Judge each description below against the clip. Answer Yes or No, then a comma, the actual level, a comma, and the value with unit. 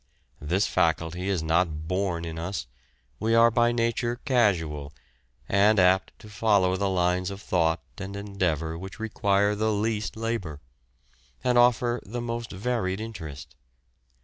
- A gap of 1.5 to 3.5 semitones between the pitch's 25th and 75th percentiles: No, average, 4.6 semitones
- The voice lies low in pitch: Yes, low, 100 Hz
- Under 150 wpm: Yes, average, 140 wpm